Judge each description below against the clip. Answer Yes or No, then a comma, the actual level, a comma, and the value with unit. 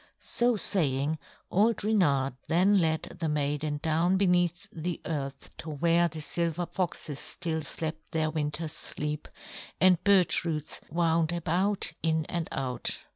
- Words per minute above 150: No, slow, 135 wpm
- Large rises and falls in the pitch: No, average, 2.7 semitones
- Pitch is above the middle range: No, medium, 165 Hz